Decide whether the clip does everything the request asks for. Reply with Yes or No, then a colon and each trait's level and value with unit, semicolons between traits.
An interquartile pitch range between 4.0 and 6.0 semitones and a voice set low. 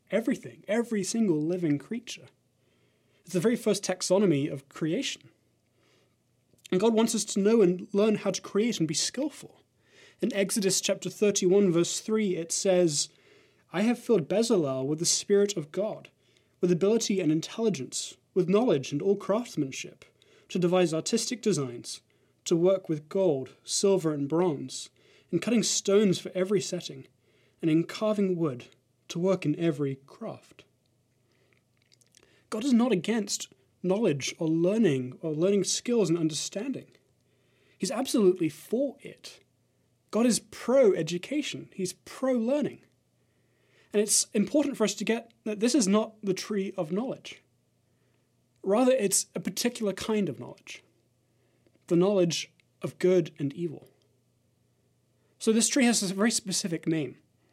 No: average, 5.3 semitones; medium, 185 Hz